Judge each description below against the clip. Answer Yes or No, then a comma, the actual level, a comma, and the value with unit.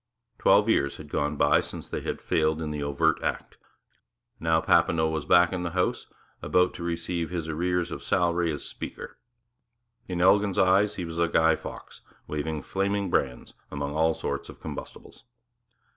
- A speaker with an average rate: Yes, average, 170 wpm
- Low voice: Yes, very low, 85 Hz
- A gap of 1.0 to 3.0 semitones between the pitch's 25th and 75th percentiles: Yes, narrow, 2.5 semitones